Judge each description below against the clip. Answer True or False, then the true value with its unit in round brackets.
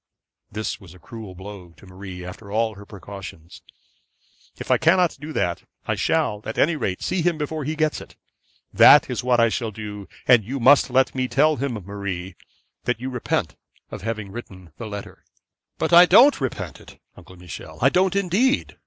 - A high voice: False (115 Hz)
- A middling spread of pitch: False (7.2 semitones)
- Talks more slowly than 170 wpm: False (185 wpm)